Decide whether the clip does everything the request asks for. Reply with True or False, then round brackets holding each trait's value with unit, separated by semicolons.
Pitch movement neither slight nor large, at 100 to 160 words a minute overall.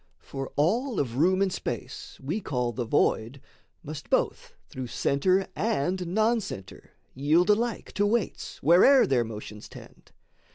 False (7.7 semitones; 140 wpm)